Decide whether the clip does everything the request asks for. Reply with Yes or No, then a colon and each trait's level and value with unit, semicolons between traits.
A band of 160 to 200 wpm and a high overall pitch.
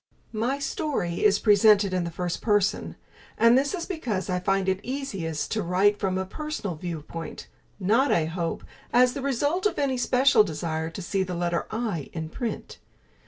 Yes: average, 175 wpm; high, 200 Hz